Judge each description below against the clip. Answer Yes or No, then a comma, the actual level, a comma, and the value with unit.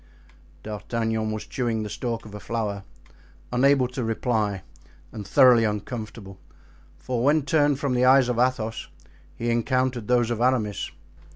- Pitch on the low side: Yes, low, 115 Hz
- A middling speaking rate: Yes, average, 145 wpm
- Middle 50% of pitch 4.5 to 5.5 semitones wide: No, average, 2.8 semitones